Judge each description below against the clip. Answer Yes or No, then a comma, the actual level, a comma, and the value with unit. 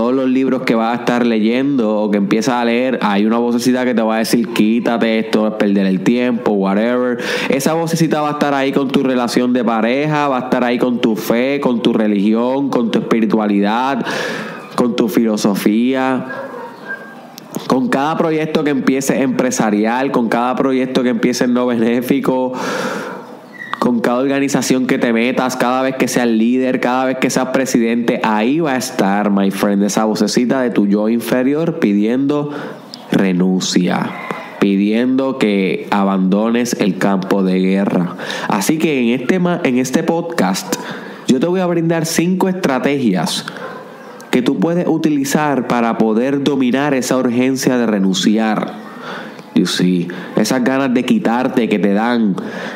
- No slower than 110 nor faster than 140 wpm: No, average, 160 wpm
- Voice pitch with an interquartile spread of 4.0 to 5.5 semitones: Yes, average, 5.1 semitones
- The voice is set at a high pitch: No, low, 125 Hz